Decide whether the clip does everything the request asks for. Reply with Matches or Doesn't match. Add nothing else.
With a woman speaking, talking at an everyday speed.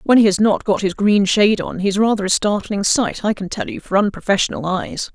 Doesn't match